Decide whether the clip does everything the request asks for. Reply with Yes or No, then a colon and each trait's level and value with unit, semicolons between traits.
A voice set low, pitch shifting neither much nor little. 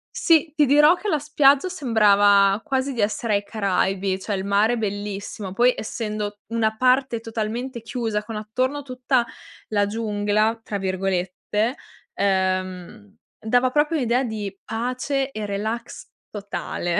No: high, 220 Hz; average, 3.8 semitones